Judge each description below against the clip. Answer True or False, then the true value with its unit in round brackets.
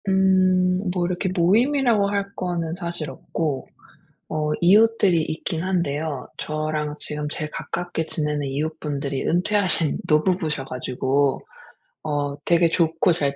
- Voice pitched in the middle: True (165 Hz)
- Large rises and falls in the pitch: False (3.6 semitones)